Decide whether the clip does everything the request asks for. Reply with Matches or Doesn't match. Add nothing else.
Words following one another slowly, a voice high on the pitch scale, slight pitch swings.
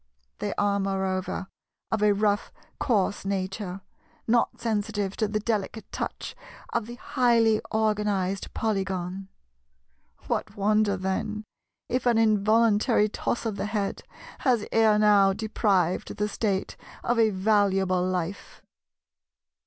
Matches